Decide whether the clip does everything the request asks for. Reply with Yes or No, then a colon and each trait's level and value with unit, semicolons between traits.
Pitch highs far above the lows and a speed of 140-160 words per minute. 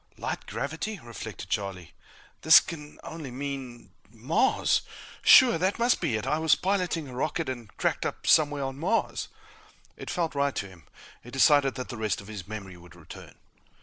No: wide, 6.7 semitones; average, 175 wpm